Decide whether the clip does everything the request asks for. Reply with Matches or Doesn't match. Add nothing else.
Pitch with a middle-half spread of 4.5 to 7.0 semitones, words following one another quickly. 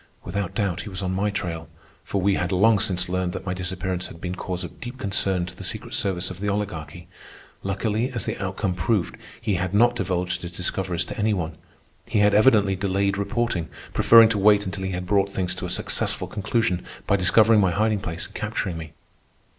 Doesn't match